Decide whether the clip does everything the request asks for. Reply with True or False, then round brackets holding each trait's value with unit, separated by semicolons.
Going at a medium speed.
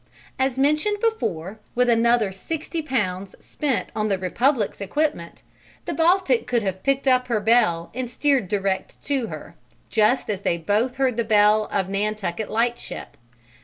True (155 wpm)